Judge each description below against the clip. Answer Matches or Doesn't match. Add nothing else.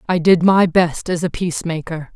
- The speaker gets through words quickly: Doesn't match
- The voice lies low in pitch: Doesn't match